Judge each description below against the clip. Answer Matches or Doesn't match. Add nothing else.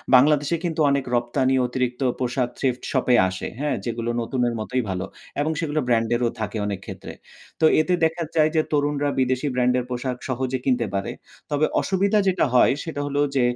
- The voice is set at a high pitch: Doesn't match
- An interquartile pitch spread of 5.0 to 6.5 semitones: Doesn't match